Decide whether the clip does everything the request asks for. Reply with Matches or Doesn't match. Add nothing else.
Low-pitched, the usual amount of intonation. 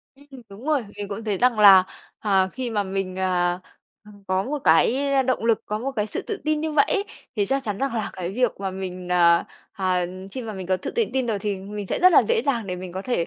Doesn't match